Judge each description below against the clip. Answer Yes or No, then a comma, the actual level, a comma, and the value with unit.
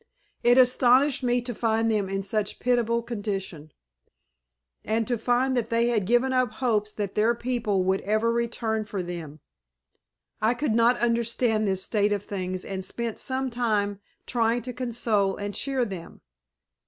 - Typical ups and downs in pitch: Yes, average, 3.0 semitones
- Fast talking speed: No, average, 165 wpm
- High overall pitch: Yes, high, 225 Hz